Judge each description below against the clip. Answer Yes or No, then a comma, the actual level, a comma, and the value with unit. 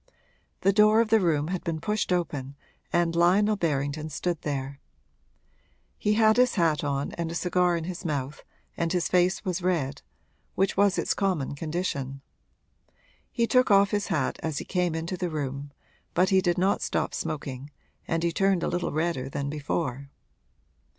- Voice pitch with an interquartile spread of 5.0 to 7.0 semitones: No, average, 4.4 semitones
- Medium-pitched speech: Yes, medium, 170 Hz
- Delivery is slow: No, average, 170 wpm